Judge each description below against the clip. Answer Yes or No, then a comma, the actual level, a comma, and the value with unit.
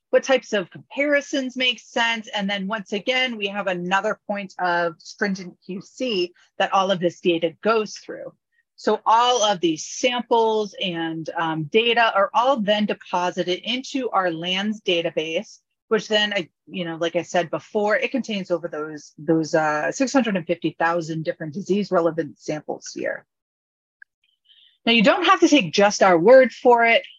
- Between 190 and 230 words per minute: No, average, 170 wpm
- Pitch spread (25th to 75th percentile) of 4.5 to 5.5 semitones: Yes, average, 5.2 semitones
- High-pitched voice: Yes, high, 200 Hz